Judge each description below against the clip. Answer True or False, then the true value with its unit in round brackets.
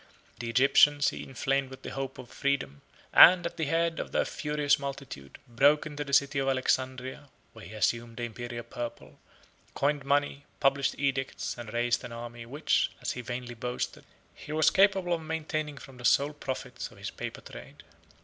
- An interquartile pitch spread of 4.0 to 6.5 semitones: False (3.3 semitones)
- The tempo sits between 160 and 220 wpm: True (180 wpm)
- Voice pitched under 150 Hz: True (135 Hz)